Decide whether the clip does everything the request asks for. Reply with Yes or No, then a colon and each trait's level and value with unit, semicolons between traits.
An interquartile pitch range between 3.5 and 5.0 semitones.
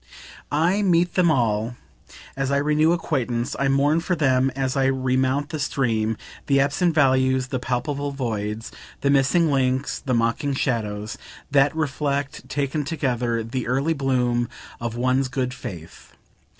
No: average, 2.7 semitones